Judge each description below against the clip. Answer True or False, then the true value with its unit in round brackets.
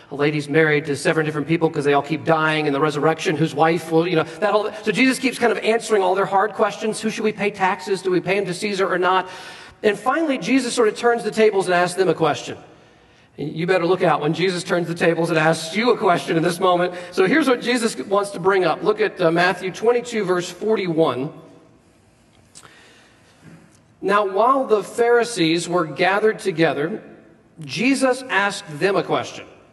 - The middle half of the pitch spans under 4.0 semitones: False (4.8 semitones)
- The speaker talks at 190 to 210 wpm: True (205 wpm)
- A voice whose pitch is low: False (185 Hz)